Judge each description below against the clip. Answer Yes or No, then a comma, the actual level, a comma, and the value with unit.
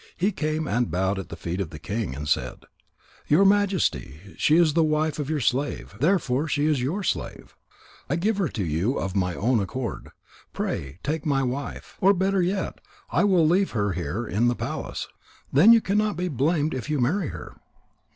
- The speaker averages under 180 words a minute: No, average, 195 wpm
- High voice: No, medium, 145 Hz